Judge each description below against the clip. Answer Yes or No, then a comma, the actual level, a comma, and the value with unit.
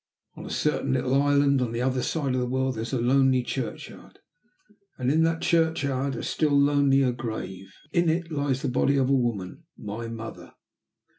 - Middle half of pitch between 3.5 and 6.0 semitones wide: No, narrow, 2.5 semitones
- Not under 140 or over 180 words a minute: No, average, 190 wpm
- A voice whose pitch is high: No, low, 135 Hz